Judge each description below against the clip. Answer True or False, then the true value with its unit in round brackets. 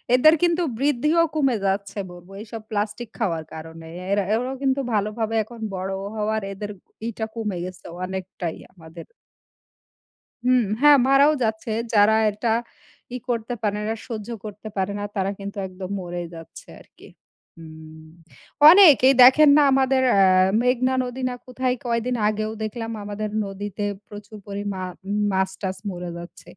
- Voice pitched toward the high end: True (215 Hz)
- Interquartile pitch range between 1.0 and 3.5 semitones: False (4.6 semitones)